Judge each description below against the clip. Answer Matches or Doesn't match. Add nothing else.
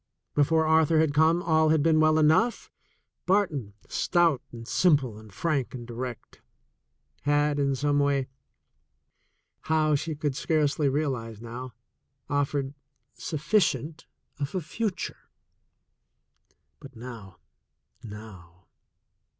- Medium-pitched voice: Matches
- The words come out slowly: Matches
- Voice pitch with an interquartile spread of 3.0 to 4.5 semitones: Matches